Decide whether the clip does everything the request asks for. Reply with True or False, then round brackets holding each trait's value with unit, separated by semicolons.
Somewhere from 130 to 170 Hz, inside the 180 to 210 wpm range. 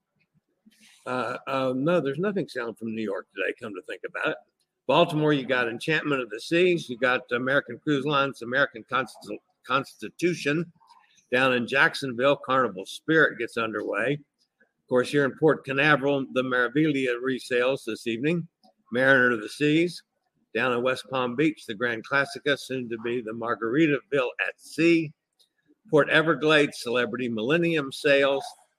False (140 Hz; 150 wpm)